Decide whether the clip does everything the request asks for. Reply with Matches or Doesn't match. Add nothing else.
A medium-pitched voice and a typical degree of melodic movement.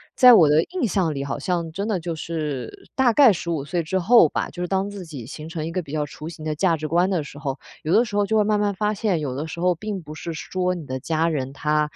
Matches